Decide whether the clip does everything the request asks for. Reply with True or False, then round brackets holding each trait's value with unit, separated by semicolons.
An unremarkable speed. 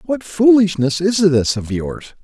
True (160 wpm)